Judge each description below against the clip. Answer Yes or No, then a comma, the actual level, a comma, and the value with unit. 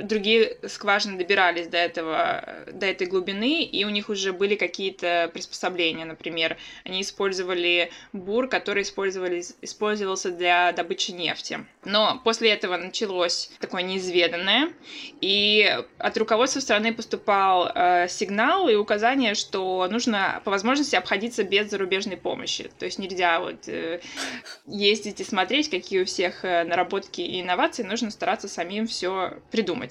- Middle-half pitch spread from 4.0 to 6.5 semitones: No, average, 3.6 semitones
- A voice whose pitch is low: No, high, 195 Hz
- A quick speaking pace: No, average, 130 wpm